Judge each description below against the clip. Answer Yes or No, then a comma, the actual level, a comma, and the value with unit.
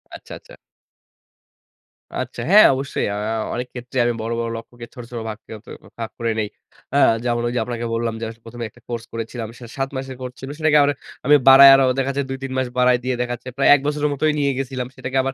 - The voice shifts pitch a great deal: No, narrow, 2.4 semitones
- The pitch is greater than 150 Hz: No, low, 125 Hz